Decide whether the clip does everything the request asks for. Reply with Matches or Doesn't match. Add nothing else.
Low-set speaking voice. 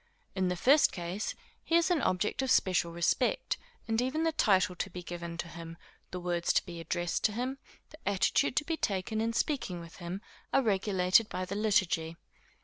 Doesn't match